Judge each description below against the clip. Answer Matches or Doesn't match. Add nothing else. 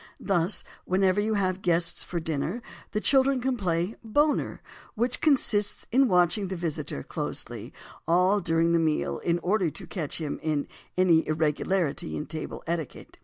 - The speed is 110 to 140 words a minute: Doesn't match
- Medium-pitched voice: Matches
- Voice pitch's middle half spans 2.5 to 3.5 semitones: Doesn't match